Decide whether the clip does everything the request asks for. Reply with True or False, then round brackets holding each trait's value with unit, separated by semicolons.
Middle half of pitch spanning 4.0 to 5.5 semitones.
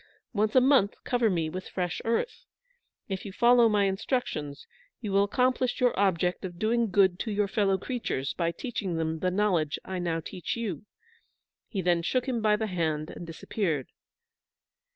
True (4.7 semitones)